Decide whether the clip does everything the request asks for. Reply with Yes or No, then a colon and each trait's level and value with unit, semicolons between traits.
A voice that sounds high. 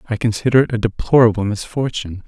No: low, 115 Hz